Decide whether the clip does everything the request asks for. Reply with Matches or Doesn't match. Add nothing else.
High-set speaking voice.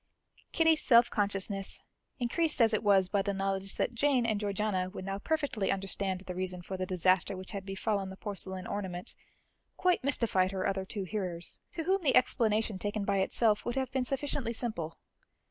Matches